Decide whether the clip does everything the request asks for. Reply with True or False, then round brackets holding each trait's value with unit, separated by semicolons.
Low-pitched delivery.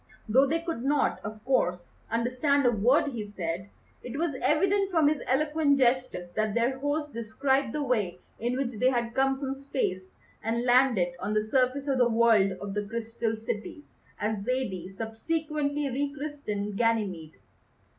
False (245 Hz)